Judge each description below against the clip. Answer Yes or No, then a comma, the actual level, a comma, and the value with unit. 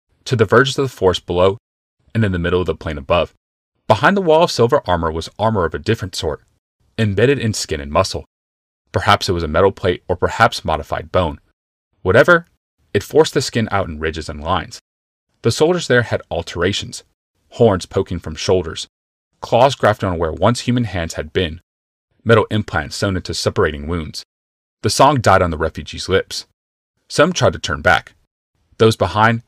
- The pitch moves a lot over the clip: Yes, wide, 6.3 semitones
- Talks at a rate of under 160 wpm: No, average, 185 wpm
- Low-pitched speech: Yes, very low, 90 Hz